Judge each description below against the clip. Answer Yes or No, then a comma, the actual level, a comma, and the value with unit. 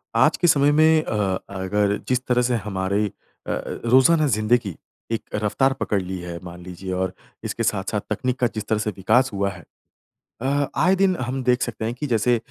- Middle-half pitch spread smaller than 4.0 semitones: No, average, 5.0 semitones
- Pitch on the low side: Yes, low, 115 Hz